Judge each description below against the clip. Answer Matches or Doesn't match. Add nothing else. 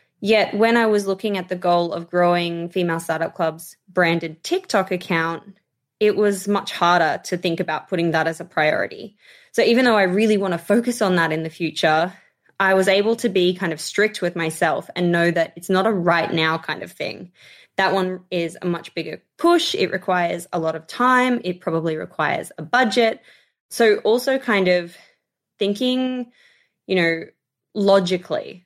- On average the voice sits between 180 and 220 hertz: Matches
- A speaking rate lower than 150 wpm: Doesn't match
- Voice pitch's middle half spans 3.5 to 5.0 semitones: Matches